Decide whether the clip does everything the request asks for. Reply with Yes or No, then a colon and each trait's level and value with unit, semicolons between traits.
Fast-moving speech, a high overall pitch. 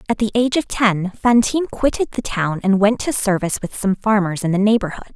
Yes: fast, 220 wpm; high, 210 Hz